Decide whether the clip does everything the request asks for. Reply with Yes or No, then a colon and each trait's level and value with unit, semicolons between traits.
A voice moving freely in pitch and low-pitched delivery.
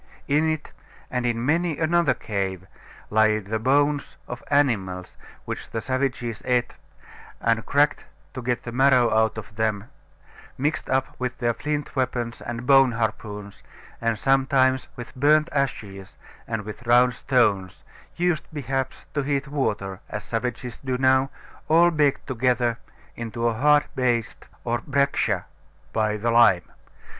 No: average, 3.7 semitones; low, 125 Hz